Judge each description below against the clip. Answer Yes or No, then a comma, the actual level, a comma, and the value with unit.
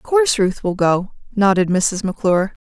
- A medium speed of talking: Yes, average, 185 wpm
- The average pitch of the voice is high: Yes, high, 200 Hz